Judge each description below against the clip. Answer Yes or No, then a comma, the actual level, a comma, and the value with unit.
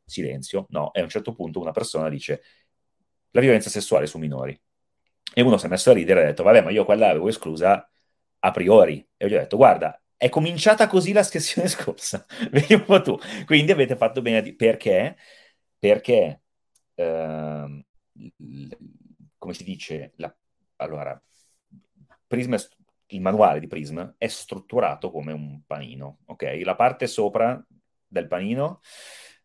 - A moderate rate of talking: Yes, average, 155 wpm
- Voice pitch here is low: Yes, low, 110 Hz